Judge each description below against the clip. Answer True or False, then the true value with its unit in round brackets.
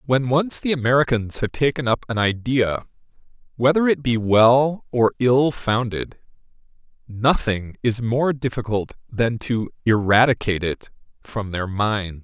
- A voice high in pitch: False (120 Hz)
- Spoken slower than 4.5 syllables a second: True (4.2 syllables/s)